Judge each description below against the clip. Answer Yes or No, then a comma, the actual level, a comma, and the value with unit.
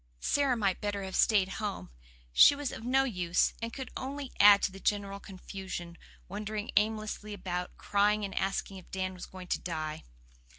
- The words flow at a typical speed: Yes, average, 175 wpm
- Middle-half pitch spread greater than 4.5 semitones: No, narrow, 2.4 semitones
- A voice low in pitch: No, high, 200 Hz